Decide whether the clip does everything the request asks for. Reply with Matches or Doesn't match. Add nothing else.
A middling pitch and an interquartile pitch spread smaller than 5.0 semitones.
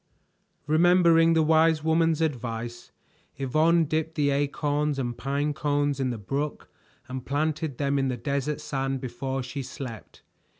Matches